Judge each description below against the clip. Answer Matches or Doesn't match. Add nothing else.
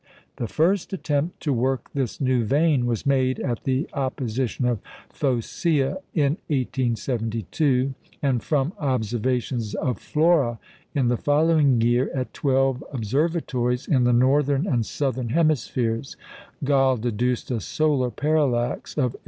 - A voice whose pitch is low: Matches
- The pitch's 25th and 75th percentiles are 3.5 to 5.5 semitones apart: Doesn't match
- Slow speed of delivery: Matches